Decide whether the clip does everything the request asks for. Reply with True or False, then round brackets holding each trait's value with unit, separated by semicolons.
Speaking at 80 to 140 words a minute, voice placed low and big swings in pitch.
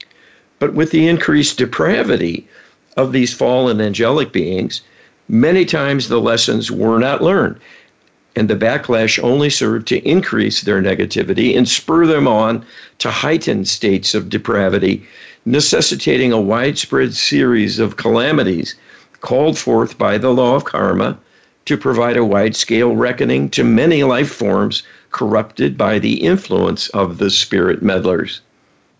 False (135 wpm; 120 Hz; 3.7 semitones)